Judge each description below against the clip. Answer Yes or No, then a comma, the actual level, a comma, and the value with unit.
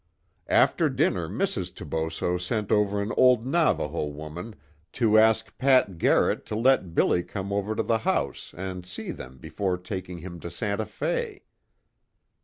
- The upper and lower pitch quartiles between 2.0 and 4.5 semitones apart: Yes, average, 4.0 semitones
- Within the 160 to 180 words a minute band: No, average, 150 wpm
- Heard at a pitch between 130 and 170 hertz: No, low, 100 Hz